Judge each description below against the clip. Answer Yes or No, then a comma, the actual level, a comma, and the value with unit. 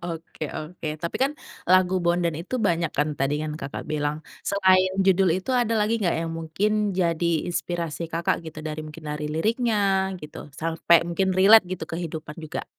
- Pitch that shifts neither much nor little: Yes, average, 3.0 semitones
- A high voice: No, medium, 170 Hz